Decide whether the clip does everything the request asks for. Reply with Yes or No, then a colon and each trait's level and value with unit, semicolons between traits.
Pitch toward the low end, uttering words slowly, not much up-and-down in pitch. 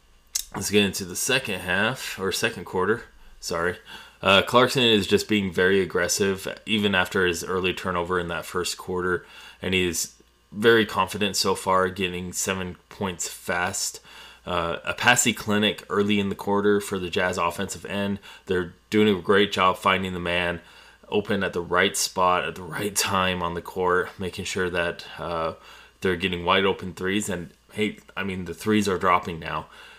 No: very low, 95 Hz; average, 175 wpm; narrow, 2.3 semitones